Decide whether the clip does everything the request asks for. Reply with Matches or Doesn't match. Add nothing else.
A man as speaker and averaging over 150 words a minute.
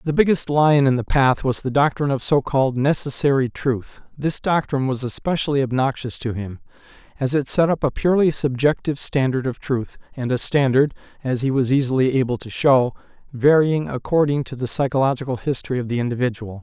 Matches